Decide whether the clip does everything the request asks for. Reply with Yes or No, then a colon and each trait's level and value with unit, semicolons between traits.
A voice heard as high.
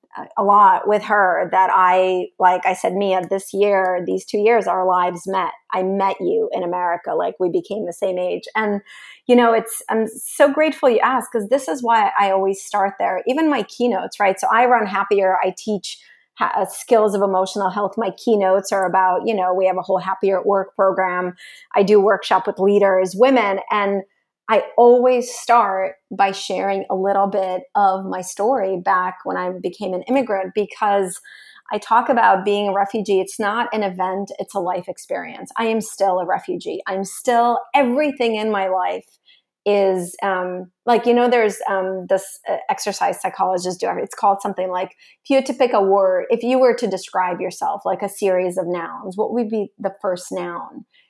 Yes: high, 195 Hz